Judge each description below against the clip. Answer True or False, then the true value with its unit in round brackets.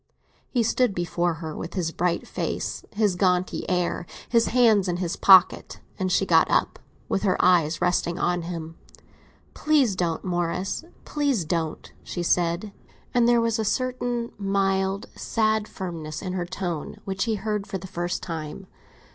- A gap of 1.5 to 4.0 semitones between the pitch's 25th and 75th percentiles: True (3.6 semitones)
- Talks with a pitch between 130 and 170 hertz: False (185 Hz)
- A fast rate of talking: False (165 wpm)